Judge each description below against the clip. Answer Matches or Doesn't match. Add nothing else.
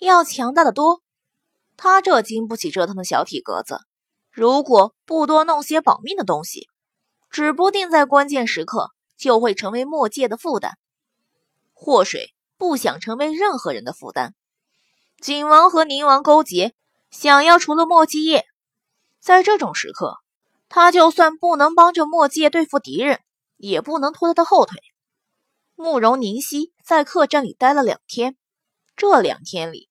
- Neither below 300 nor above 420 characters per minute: Doesn't match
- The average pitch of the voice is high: Matches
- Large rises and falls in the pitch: Doesn't match